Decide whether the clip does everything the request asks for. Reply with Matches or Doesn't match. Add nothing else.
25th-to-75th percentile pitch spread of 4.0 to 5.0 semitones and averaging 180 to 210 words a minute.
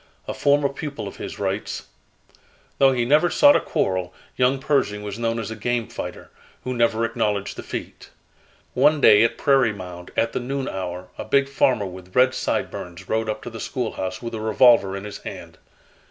Matches